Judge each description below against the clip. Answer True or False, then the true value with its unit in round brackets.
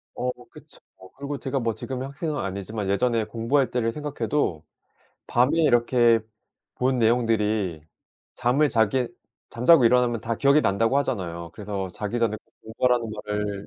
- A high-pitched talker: False (115 Hz)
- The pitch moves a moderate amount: True (3.7 semitones)